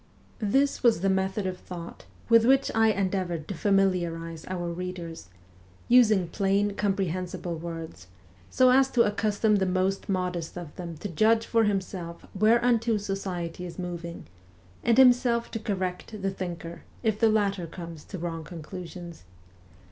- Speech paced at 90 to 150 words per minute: Yes, average, 145 wpm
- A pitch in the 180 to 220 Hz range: Yes, high, 190 Hz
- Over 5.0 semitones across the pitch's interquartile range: No, average, 3.9 semitones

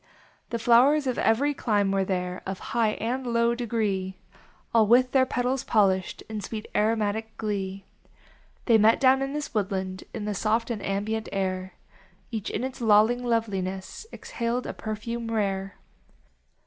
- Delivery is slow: No, average, 150 wpm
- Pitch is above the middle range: Yes, high, 220 Hz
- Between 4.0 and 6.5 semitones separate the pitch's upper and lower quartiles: No, average, 3.3 semitones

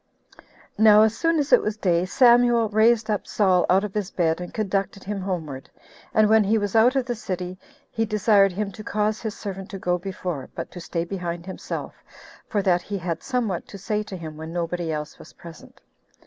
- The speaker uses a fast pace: Yes, fast, 210 wpm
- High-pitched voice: Yes, high, 195 Hz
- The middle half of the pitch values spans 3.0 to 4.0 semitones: Yes, average, 3.4 semitones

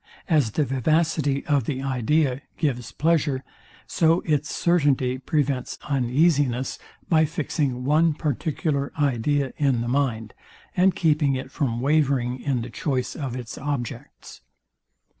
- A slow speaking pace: Yes, slow, 125 wpm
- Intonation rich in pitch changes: No, average, 3.2 semitones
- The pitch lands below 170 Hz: Yes, medium, 140 Hz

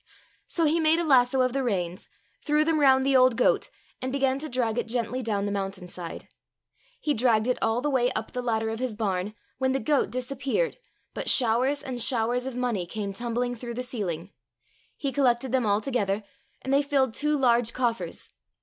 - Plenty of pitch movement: No, average, 3.3 semitones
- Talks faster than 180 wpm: Yes, average, 200 wpm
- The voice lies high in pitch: Yes, high, 245 Hz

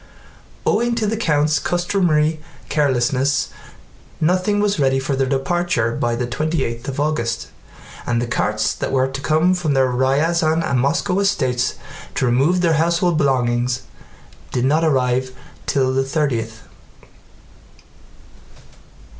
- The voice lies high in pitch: No, medium, 140 Hz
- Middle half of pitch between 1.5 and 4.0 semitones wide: No, average, 4.5 semitones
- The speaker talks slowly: Yes, slow, 130 wpm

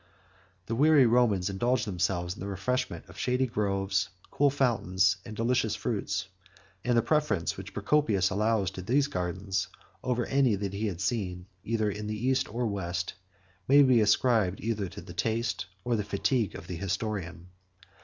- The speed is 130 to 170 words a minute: Yes, average, 165 wpm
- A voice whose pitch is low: Yes, low, 105 Hz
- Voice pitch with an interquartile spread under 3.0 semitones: No, average, 4.2 semitones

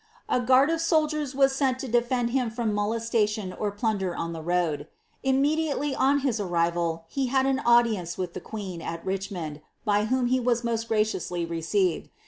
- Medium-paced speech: Yes, average, 180 wpm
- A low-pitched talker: No, high, 225 Hz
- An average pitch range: No, wide, 6.3 semitones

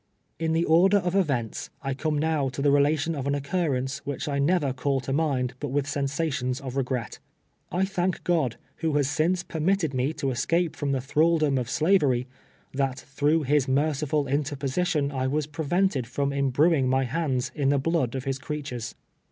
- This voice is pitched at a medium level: Yes, medium, 145 Hz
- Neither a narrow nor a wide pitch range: Yes, average, 3.2 semitones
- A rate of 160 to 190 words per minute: Yes, average, 185 wpm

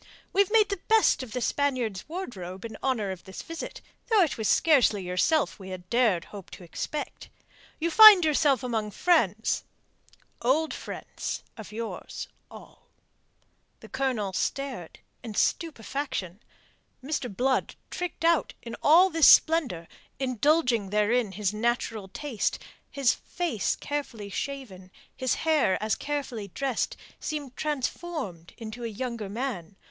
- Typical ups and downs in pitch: No, wide, 6.3 semitones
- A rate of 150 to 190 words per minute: No, slow, 135 wpm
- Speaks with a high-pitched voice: Yes, high, 245 Hz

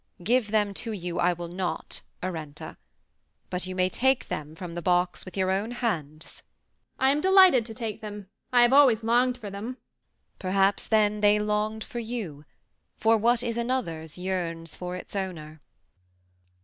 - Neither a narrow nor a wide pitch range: Yes, average, 4.7 semitones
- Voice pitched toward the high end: Yes, high, 205 Hz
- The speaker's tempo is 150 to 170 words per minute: Yes, average, 165 wpm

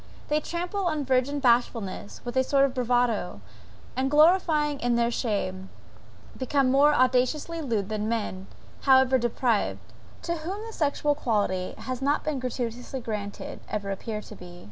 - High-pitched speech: Yes, very high, 255 Hz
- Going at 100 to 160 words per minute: Yes, average, 150 wpm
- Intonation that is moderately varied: Yes, average, 4.7 semitones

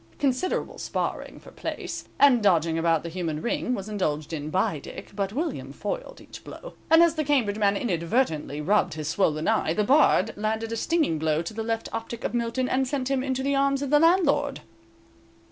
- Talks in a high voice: Yes, high, 225 Hz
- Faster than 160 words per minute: Yes, average, 195 wpm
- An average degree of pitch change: No, wide, 8.5 semitones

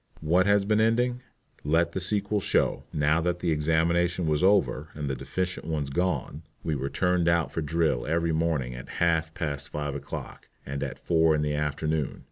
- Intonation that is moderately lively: Yes, average, 3.0 semitones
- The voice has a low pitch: Yes, very low, 80 Hz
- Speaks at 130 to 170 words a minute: No, average, 190 wpm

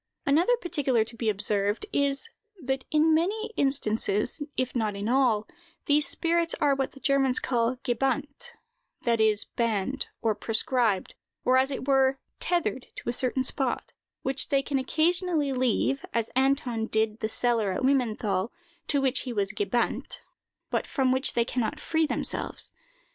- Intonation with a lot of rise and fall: No, average, 3.8 semitones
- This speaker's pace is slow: No, average, 160 wpm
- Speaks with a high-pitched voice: Yes, very high, 260 Hz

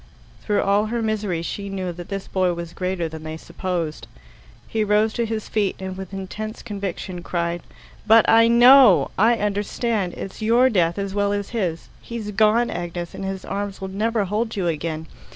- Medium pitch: No, high, 200 Hz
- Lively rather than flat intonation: No, average, 3.5 semitones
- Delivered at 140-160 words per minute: No, average, 185 wpm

